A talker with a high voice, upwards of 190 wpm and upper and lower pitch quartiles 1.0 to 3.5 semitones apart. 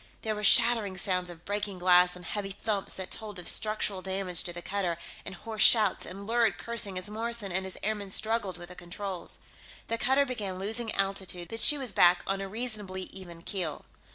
Yes: high, 195 Hz; average, 200 wpm; average, 3.0 semitones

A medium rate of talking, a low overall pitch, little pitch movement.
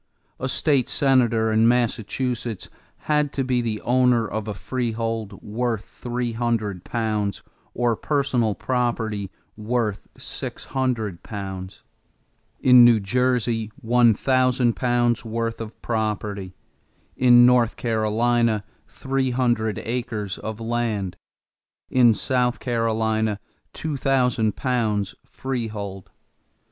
No: slow, 110 wpm; low, 115 Hz; narrow, 2.3 semitones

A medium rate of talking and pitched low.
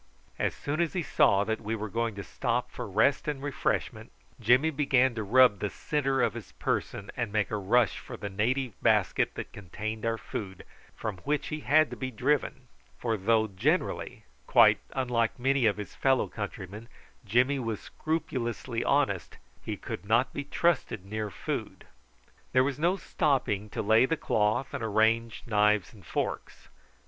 Yes: average, 170 wpm; low, 115 Hz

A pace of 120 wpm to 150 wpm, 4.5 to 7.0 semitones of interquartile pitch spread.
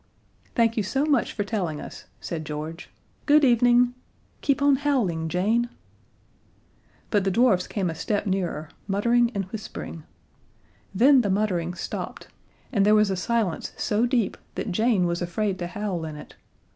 No: average, 160 wpm; average, 5.0 semitones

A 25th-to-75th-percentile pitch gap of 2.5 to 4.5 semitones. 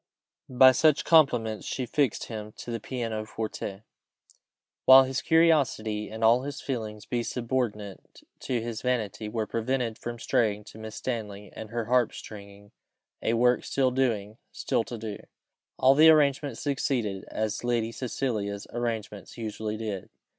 Yes: average, 3.1 semitones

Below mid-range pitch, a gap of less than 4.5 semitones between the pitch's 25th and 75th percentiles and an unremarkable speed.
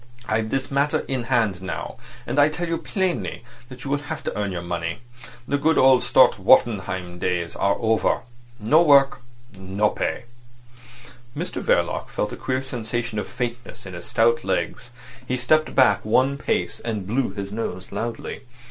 No: low, 115 Hz; average, 5.1 semitones; average, 170 wpm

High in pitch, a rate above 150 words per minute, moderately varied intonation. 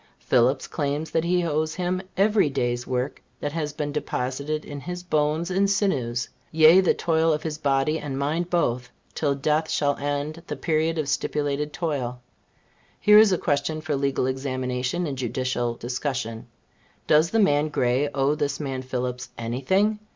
No: medium, 145 Hz; average, 165 wpm; average, 3.7 semitones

